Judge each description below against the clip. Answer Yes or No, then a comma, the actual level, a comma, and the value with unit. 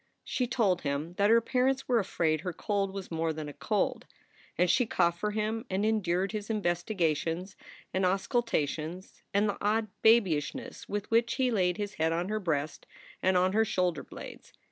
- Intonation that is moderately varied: Yes, average, 4.2 semitones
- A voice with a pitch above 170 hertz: Yes, high, 190 Hz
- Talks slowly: No, average, 180 wpm